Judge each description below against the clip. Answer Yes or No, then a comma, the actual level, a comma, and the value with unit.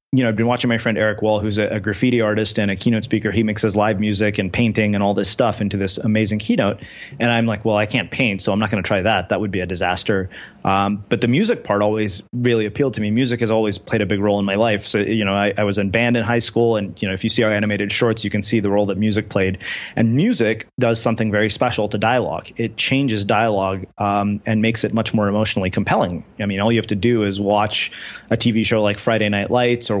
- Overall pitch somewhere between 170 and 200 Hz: No, low, 110 Hz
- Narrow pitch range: Yes, narrow, 2.0 semitones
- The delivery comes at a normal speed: No, fast, 270 wpm